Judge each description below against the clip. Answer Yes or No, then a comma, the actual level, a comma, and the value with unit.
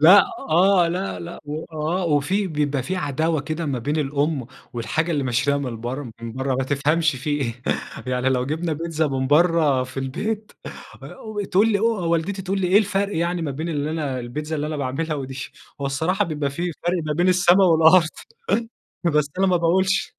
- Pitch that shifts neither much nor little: Yes, average, 4.1 semitones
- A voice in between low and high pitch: Yes, medium, 155 Hz